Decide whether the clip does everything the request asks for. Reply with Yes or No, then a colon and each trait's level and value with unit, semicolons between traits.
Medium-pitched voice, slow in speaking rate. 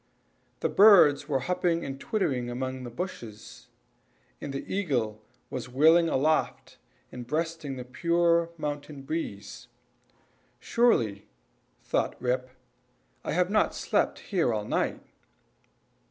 Yes: medium, 145 Hz; slow, 115 wpm